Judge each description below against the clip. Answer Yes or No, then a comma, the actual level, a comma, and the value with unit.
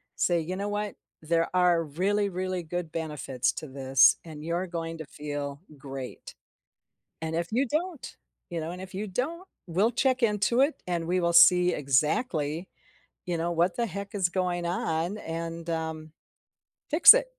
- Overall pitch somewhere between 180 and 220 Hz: No, medium, 170 Hz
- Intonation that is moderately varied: Yes, average, 3.8 semitones